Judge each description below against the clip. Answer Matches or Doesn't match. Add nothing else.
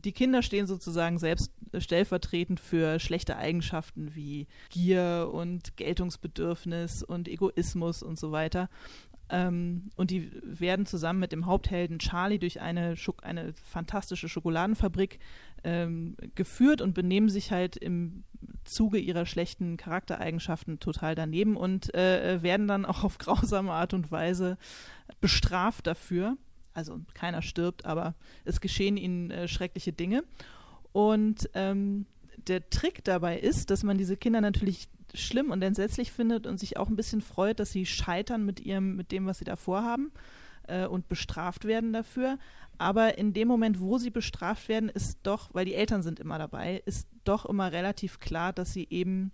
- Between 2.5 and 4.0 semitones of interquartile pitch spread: Matches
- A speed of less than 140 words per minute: Doesn't match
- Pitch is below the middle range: Doesn't match